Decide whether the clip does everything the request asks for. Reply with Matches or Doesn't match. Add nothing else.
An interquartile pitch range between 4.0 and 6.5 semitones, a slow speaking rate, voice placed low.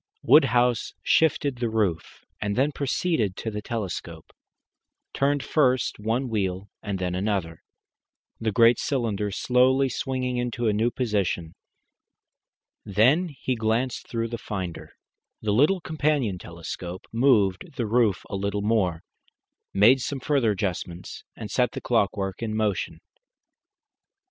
Matches